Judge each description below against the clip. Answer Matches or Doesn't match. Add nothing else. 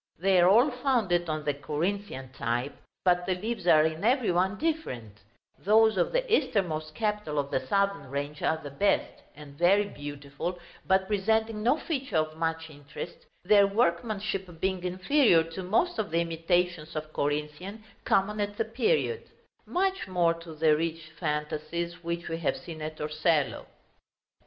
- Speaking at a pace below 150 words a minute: Doesn't match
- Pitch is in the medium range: Matches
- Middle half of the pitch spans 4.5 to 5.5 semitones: Matches